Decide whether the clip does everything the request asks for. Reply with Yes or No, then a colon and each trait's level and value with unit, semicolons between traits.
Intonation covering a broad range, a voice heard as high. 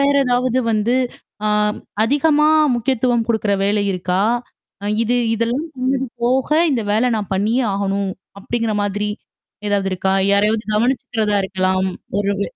No: average, 3.8 semitones; high, 220 Hz